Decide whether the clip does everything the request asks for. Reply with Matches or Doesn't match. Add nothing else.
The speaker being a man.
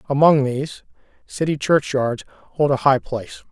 Matches